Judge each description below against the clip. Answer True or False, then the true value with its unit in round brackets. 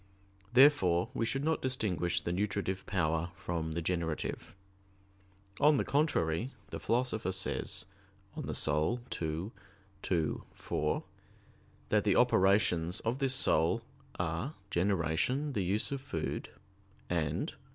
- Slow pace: True (120 wpm)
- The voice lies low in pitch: True (95 Hz)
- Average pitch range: False (6.9 semitones)